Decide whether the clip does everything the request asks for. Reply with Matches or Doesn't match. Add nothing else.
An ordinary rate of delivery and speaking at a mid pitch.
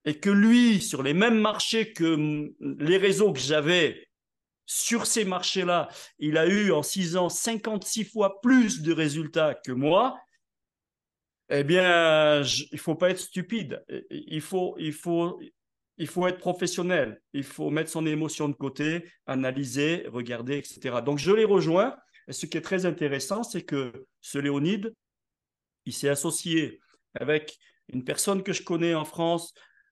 Matches